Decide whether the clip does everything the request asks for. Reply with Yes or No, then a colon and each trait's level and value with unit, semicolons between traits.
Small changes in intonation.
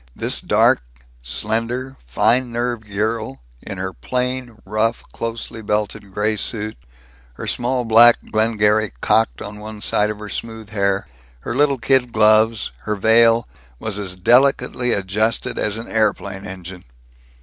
Yes: narrow, 2.2 semitones